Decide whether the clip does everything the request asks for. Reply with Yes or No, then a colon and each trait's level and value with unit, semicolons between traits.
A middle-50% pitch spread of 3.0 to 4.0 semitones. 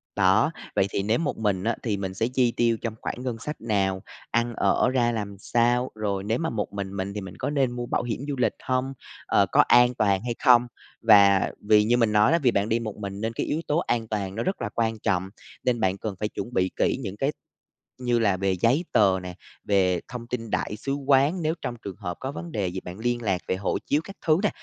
Yes: average, 3.7 semitones